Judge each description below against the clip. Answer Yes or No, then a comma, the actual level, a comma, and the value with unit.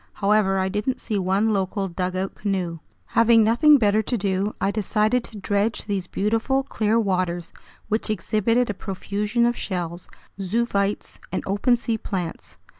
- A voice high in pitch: Yes, high, 205 Hz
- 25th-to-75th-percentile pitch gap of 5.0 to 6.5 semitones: No, average, 2.9 semitones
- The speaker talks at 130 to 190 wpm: Yes, average, 150 wpm